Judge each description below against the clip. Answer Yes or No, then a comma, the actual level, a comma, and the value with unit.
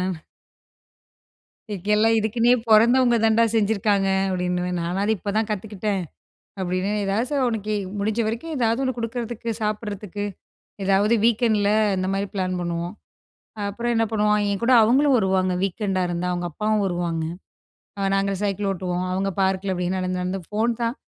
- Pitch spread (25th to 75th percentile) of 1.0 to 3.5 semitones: Yes, average, 3.1 semitones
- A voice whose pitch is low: No, high, 205 Hz